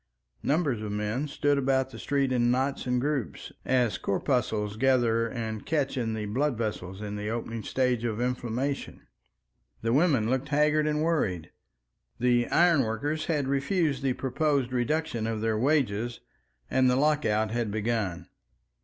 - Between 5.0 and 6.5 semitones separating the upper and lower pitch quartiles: No, average, 4.2 semitones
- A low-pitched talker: Yes, low, 125 Hz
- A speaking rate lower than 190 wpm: Yes, average, 150 wpm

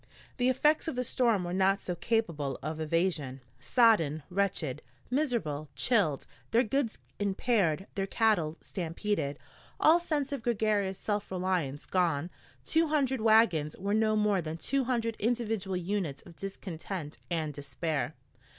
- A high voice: Yes, high, 195 Hz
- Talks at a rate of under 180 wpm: Yes, average, 140 wpm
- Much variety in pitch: Yes, wide, 6.1 semitones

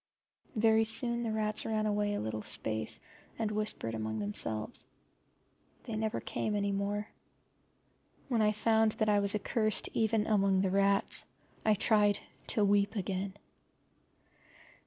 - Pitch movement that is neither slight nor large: No, narrow, 1.8 semitones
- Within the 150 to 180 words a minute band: No, slow, 135 wpm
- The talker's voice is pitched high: Yes, high, 210 Hz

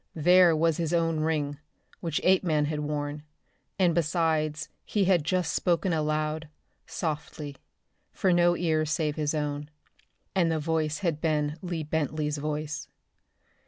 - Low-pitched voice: No, medium, 155 Hz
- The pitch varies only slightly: Yes, narrow, 2.1 semitones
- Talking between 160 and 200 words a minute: No, slow, 135 wpm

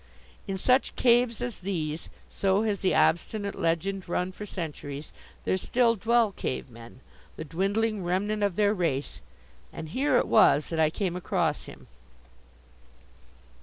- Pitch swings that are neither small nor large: Yes, average, 4.6 semitones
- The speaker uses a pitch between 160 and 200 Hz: Yes, high, 190 Hz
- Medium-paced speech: Yes, average, 145 wpm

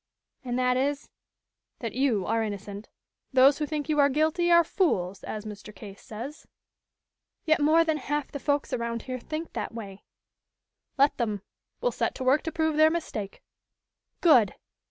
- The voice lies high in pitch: Yes, very high, 265 Hz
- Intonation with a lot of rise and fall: Yes, wide, 5.8 semitones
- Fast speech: No, average, 170 wpm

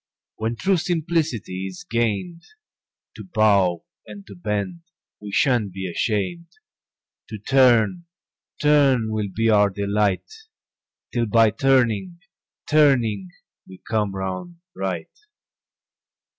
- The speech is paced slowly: Yes, slow, 105 wpm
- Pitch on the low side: Yes, low, 110 Hz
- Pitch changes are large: Yes, wide, 5.7 semitones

